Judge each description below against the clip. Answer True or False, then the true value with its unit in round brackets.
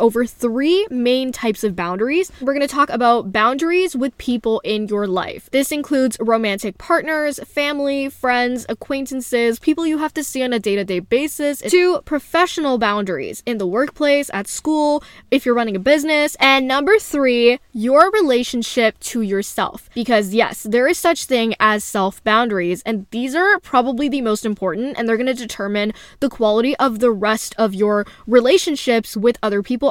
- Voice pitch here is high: True (245 Hz)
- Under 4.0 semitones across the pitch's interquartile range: False (4.5 semitones)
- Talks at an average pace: True (170 wpm)